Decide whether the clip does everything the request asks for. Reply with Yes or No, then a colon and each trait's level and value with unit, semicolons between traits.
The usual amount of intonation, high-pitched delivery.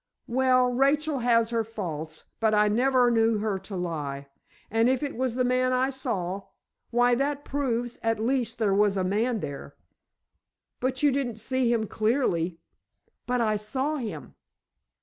Yes: average, 3.6 semitones; high, 235 Hz